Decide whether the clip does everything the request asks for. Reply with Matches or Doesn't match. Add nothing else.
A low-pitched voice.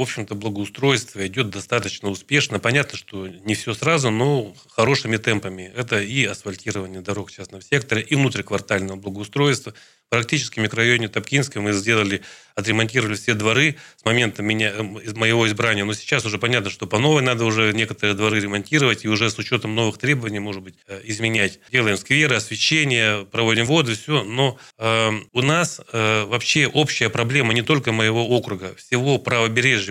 Matches